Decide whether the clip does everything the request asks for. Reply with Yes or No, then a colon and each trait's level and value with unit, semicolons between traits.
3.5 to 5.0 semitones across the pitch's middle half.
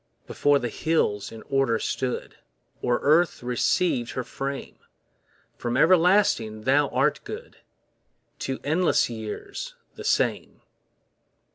No: wide, 5.4 semitones